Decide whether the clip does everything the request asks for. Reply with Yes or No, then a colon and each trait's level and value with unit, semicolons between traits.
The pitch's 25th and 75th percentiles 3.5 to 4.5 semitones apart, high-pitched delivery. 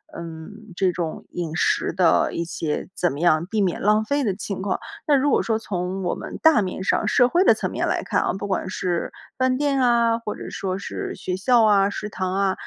Yes: average, 4.2 semitones; high, 195 Hz